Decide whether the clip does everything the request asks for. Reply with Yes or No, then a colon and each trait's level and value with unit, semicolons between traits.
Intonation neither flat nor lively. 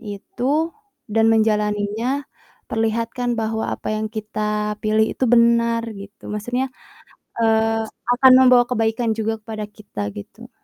No: narrow, 1.7 semitones